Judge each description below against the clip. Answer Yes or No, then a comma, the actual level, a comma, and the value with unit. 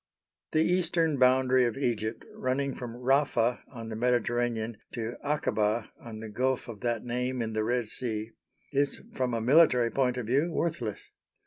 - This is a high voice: No, low, 125 Hz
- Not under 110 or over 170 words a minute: Yes, average, 160 wpm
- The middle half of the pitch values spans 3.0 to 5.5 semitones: No, narrow, 2.6 semitones